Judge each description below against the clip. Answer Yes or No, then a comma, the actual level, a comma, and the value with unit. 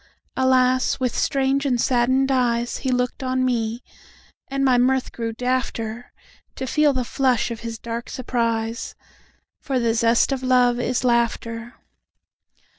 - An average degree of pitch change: No, narrow, 1.8 semitones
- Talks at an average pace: No, slow, 125 wpm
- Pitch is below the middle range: No, very high, 250 Hz